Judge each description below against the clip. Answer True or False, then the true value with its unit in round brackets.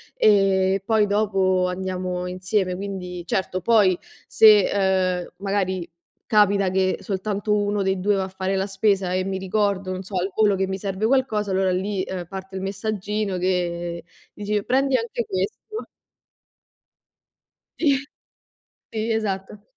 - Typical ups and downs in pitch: False (1.9 semitones)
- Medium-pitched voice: False (195 Hz)